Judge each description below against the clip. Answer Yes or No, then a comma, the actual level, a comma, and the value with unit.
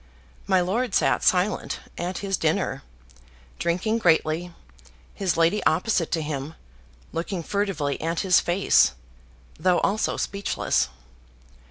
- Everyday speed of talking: No, slow, 115 wpm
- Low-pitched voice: No, medium, 180 Hz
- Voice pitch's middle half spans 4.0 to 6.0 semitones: No, average, 3.2 semitones